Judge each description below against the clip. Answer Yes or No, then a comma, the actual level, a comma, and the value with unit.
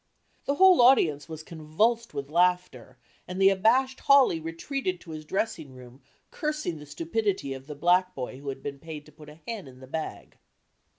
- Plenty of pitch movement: Yes, wide, 6.9 semitones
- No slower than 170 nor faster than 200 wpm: Yes, average, 185 wpm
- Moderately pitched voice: Yes, medium, 165 Hz